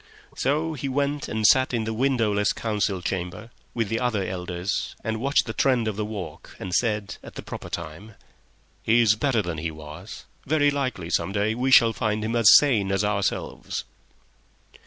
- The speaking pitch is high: No, low, 110 Hz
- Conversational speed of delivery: Yes, average, 180 wpm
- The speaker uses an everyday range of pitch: Yes, average, 4.2 semitones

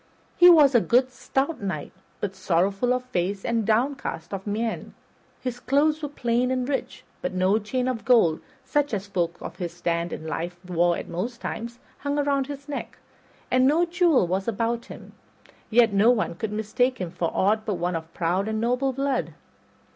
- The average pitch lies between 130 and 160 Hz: No, high, 230 Hz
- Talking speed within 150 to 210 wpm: Yes, average, 185 wpm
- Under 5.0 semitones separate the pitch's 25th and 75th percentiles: No, wide, 5.6 semitones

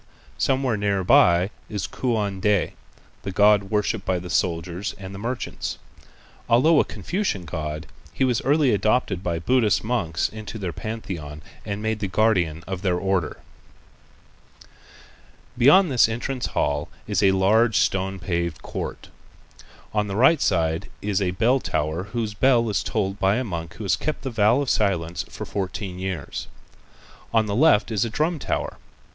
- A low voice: Yes, low, 100 Hz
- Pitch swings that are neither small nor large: Yes, average, 4.3 semitones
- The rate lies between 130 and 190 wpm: Yes, average, 160 wpm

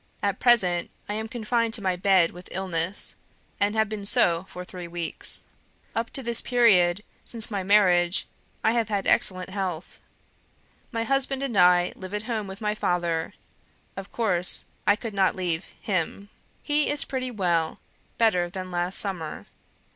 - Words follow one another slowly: No, average, 160 wpm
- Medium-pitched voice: No, high, 195 Hz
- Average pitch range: Yes, average, 3.8 semitones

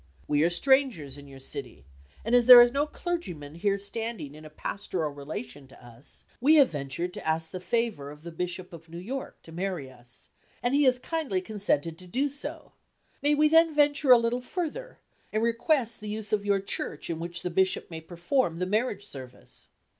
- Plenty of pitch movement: Yes, wide, 7.6 semitones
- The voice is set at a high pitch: Yes, high, 195 Hz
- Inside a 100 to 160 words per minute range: No, average, 200 wpm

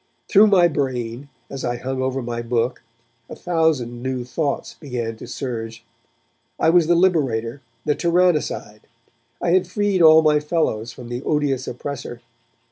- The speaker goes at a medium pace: Yes, average, 150 wpm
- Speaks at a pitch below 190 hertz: Yes, low, 135 Hz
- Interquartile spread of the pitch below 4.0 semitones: No, average, 5.3 semitones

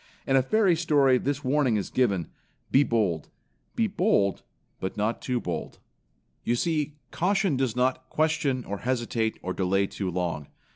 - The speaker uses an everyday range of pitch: No, wide, 6.7 semitones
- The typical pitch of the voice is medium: No, low, 130 Hz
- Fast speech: No, average, 155 wpm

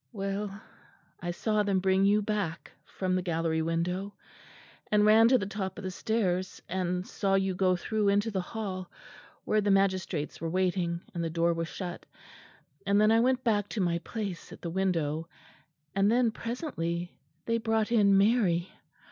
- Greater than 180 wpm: No, average, 175 wpm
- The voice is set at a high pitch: Yes, high, 195 Hz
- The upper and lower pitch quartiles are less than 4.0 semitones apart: Yes, average, 3.2 semitones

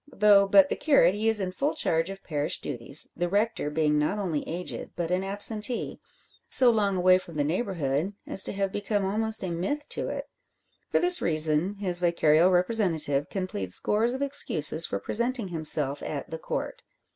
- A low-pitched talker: No, medium, 185 Hz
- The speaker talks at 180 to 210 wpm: Yes, average, 185 wpm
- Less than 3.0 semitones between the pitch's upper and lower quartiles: No, average, 4.8 semitones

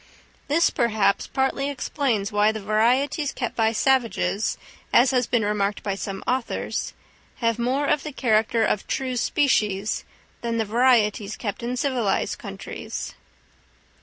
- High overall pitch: Yes, high, 235 Hz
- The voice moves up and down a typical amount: Yes, average, 3.7 semitones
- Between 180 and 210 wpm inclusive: No, slow, 135 wpm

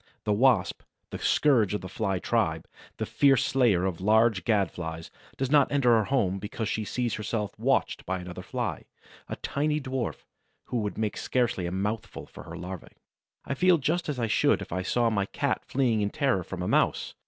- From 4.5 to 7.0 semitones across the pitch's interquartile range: Yes, wide, 5.4 semitones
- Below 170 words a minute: No, average, 200 wpm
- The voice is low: Yes, low, 110 Hz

